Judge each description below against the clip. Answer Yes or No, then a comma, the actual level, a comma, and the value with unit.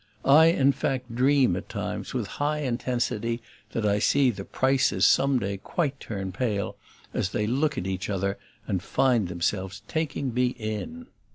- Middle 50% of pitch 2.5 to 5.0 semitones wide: No, wide, 5.5 semitones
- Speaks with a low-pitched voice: Yes, low, 120 Hz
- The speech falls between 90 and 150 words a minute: No, average, 165 wpm